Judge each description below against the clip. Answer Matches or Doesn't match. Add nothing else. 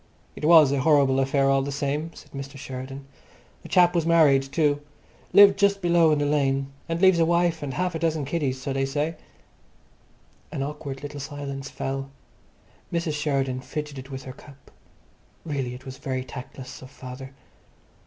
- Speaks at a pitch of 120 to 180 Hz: Matches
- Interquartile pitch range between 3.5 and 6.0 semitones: Doesn't match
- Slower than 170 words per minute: Doesn't match